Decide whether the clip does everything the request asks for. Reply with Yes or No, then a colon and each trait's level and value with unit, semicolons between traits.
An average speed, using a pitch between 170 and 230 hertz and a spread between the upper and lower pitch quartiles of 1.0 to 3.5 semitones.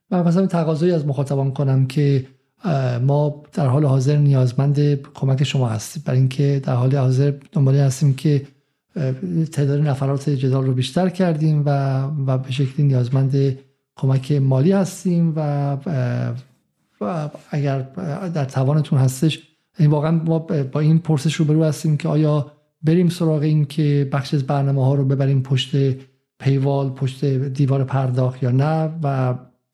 No: average, 145 wpm; medium, 140 Hz; narrow, 2.4 semitones